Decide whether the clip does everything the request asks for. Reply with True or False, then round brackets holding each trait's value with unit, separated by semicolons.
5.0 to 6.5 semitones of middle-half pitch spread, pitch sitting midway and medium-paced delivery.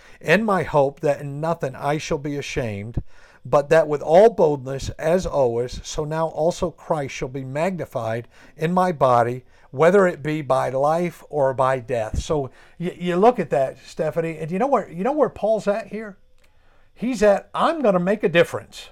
True (5.4 semitones; 155 Hz; 185 wpm)